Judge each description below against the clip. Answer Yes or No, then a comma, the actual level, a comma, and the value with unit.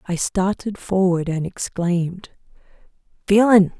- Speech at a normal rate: No, slow, 95 wpm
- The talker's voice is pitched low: No, medium, 185 Hz